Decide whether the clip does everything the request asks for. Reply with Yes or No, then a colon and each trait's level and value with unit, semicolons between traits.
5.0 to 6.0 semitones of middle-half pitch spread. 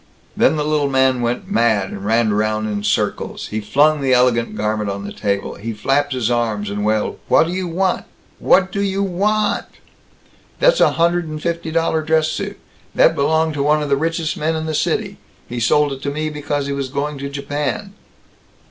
Yes: wide, 5.5 semitones